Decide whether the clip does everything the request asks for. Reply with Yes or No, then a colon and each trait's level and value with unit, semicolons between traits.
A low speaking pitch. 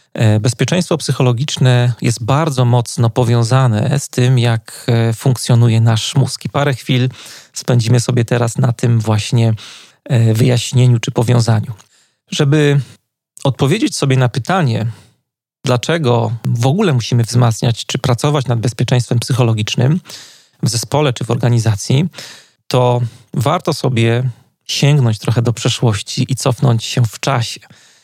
Yes: low, 125 Hz